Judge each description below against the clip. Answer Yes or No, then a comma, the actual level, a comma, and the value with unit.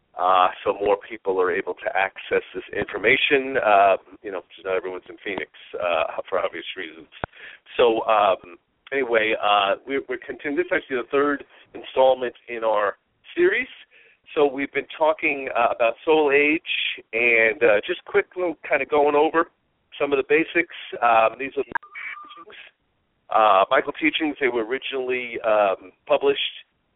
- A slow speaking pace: No, average, 155 wpm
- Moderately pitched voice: Yes, medium, 165 Hz